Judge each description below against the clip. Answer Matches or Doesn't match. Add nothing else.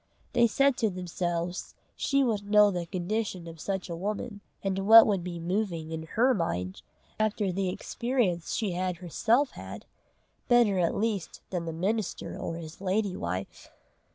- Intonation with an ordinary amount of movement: Matches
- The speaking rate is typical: Matches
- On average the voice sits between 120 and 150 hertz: Doesn't match